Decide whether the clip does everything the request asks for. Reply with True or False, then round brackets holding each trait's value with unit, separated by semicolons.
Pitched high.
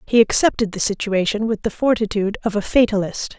True (210 Hz)